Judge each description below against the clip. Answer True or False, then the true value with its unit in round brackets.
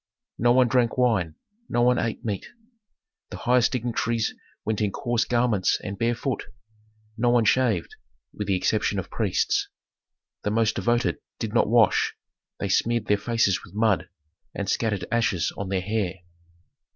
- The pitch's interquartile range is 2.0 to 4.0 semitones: True (3.0 semitones)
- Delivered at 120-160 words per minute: True (150 wpm)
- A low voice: True (115 Hz)